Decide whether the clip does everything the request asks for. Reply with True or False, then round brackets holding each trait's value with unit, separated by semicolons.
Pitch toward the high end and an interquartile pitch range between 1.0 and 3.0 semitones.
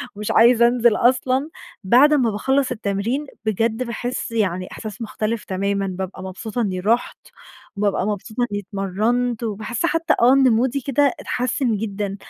False (225 Hz; 3.6 semitones)